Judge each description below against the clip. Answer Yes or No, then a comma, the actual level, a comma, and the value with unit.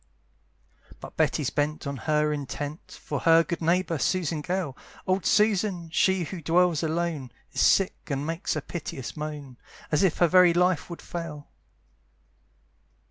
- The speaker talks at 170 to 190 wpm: No, average, 145 wpm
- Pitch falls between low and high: Yes, medium, 165 Hz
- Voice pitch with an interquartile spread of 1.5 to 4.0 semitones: Yes, average, 3.2 semitones